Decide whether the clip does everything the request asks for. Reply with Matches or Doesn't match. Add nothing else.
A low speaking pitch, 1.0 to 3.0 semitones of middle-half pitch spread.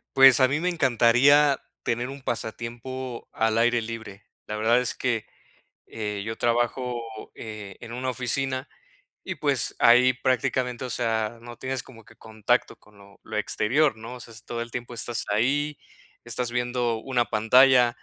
Matches